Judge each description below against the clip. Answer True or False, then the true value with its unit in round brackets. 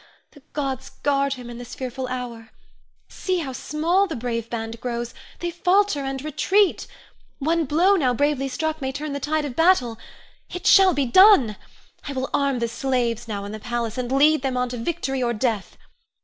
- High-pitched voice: True (270 Hz)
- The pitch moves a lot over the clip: False (4.4 semitones)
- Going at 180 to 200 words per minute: True (190 wpm)